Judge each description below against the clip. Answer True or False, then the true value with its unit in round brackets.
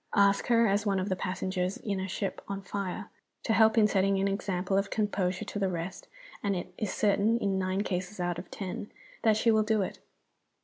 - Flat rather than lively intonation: True (2.1 semitones)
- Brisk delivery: True (215 wpm)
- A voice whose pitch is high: True (195 Hz)